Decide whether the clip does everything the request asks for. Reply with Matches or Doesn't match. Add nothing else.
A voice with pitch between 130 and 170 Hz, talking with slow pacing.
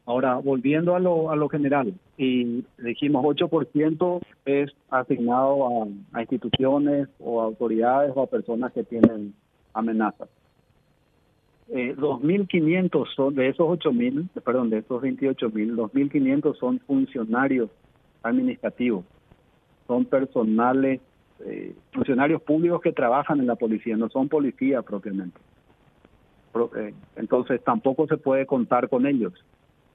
Matches